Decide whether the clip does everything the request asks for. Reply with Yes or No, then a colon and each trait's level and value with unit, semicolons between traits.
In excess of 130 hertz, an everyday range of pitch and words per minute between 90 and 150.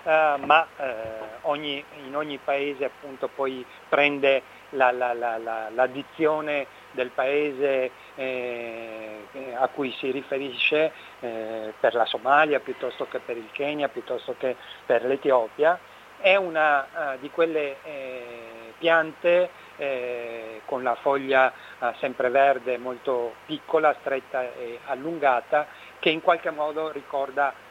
Yes: medium, 140 Hz; average, 3.5 semitones; average, 130 wpm